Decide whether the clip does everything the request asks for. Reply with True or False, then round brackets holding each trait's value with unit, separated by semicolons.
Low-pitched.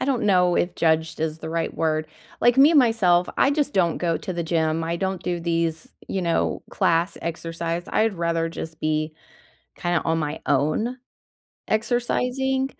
False (170 Hz)